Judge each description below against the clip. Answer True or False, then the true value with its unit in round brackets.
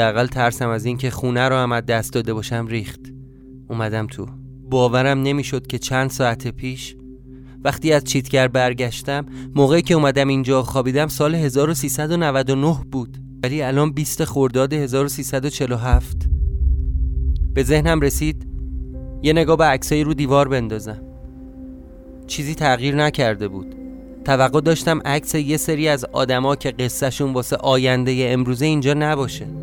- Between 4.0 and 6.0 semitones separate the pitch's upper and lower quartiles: False (3.0 semitones)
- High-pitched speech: False (130 Hz)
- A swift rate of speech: False (130 wpm)